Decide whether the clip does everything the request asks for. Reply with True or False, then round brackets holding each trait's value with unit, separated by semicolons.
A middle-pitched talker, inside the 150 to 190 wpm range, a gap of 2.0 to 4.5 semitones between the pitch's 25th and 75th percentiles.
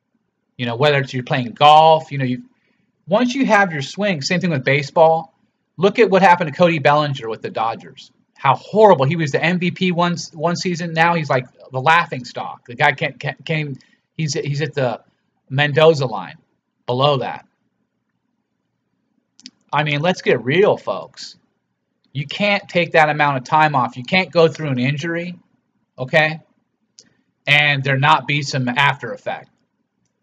True (155 Hz; 170 wpm; 3.9 semitones)